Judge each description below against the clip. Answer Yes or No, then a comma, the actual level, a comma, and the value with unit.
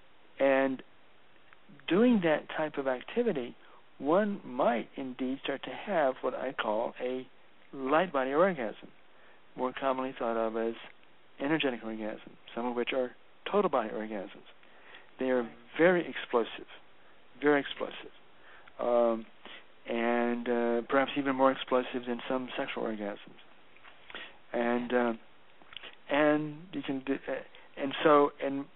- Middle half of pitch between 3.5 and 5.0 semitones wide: No, average, 2.8 semitones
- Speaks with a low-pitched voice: Yes, low, 130 Hz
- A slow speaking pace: Yes, slow, 125 wpm